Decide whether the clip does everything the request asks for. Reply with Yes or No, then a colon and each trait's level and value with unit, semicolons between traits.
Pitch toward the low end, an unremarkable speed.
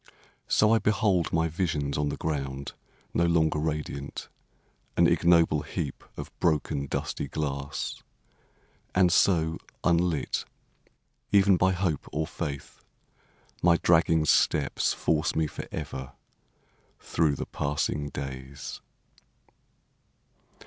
No: very low, 80 Hz; slow, 105 wpm